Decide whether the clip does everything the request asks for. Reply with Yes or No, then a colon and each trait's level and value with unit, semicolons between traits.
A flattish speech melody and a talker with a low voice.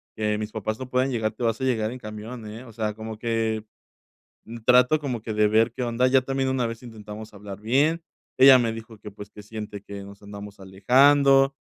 No: average, 3.0 semitones; low, 115 Hz